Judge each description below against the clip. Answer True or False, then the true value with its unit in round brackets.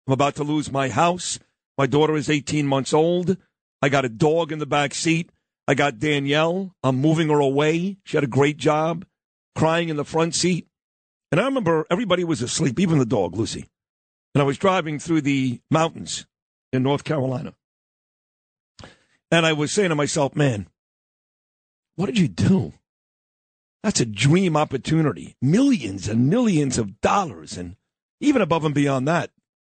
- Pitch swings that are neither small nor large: True (3.3 semitones)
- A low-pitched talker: False (150 Hz)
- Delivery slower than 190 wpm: True (165 wpm)